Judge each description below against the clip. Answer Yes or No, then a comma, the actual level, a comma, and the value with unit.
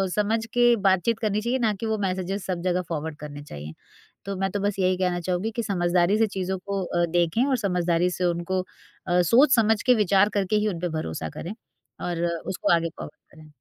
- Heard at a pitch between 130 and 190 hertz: Yes, medium, 185 Hz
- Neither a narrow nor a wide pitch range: Yes, average, 3.5 semitones